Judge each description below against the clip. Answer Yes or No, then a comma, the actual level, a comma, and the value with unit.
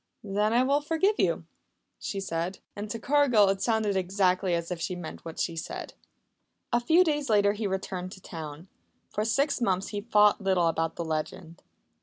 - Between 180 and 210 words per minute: Yes, average, 185 wpm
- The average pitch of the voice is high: Yes, high, 200 Hz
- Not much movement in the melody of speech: No, average, 4.2 semitones